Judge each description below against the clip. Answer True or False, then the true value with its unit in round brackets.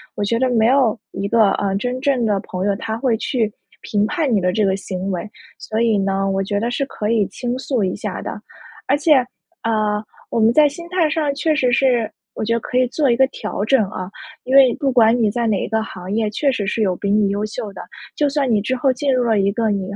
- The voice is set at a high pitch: True (225 Hz)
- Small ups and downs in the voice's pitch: False (4.2 semitones)